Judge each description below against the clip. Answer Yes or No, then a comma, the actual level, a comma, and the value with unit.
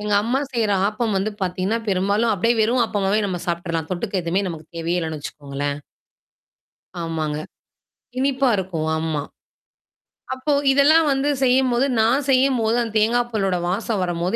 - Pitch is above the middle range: Yes, high, 205 Hz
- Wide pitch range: Yes, wide, 5.7 semitones